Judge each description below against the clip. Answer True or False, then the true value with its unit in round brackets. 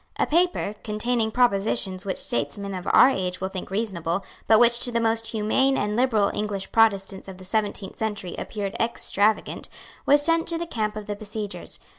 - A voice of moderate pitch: False (210 Hz)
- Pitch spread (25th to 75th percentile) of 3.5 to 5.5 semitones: False (3.0 semitones)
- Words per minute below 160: False (180 wpm)